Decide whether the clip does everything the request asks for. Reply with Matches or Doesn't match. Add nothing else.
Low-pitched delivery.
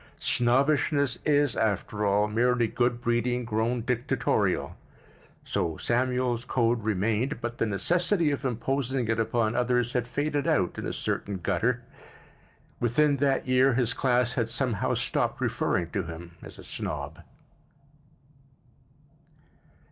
Matches